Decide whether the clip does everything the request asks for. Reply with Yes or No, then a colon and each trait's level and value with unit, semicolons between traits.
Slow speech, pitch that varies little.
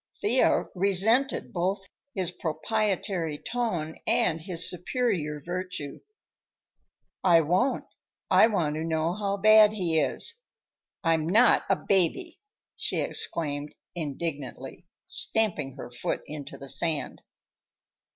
No: slow, 110 wpm; average, 4.8 semitones